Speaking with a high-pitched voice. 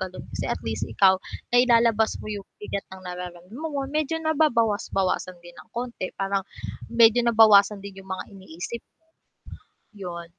Yes: high, 200 Hz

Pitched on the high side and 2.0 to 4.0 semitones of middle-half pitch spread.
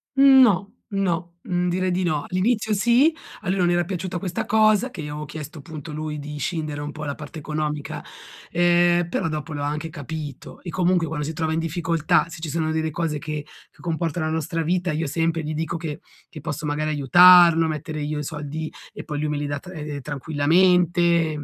No: medium, 160 Hz; average, 2.7 semitones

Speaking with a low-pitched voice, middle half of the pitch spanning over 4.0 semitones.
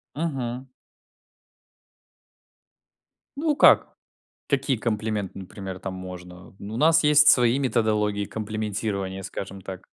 Yes: low, 110 Hz; average, 5.1 semitones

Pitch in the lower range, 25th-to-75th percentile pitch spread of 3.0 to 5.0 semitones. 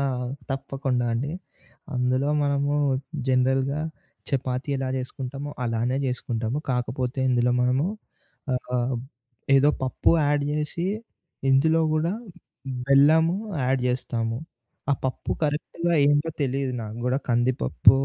No: low, 130 Hz; narrow, 2.4 semitones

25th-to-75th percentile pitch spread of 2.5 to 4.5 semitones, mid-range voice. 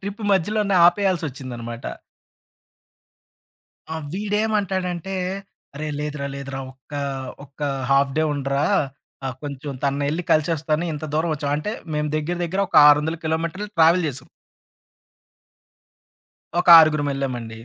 Yes: average, 4.1 semitones; medium, 155 Hz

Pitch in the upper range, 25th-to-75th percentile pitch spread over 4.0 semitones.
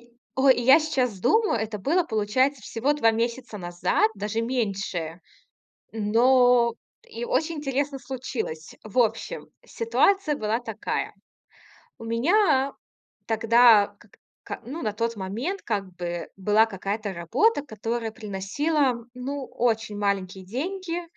Yes: high, 230 Hz; average, 4.6 semitones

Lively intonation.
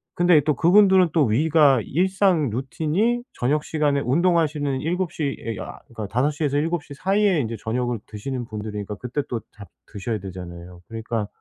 Yes: wide, 6.6 semitones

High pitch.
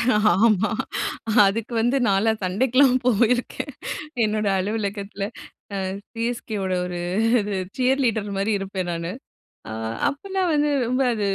Yes: high, 215 Hz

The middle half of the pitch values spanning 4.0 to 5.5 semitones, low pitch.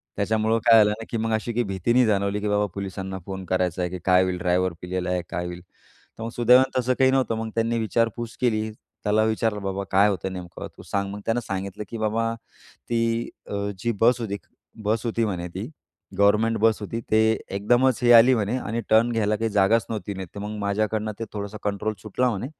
No: average, 2.7 semitones; low, 105 Hz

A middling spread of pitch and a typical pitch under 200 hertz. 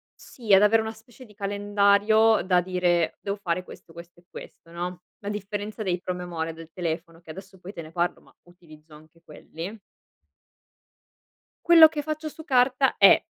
Yes: average, 4.1 semitones; high, 190 Hz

